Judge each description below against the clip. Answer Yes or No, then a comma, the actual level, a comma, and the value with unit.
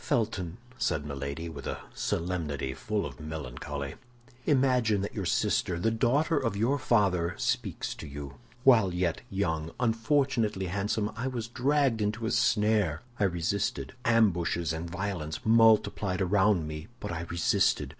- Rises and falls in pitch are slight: No, wide, 5.6 semitones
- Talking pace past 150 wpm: No, average, 145 wpm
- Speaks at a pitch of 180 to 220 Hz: No, low, 100 Hz